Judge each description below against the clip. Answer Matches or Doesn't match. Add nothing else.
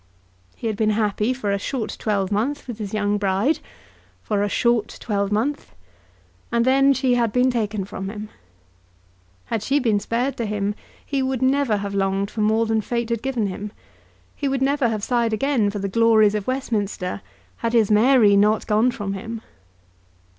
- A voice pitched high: Matches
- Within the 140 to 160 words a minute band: Doesn't match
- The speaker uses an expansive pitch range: Doesn't match